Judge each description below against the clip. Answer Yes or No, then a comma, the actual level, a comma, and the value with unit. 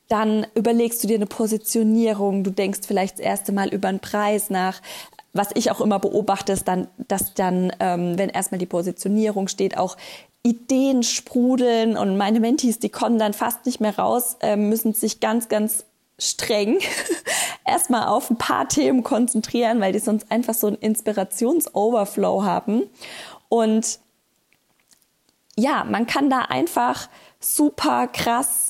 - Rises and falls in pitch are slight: No, average, 3.1 semitones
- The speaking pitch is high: Yes, high, 220 Hz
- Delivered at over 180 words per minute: No, average, 150 wpm